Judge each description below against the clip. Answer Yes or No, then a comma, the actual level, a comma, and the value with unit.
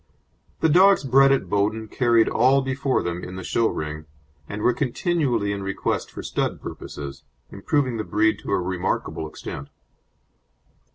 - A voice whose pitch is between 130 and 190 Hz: No, low, 110 Hz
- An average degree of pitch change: No, wide, 6.2 semitones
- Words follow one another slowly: No, average, 155 wpm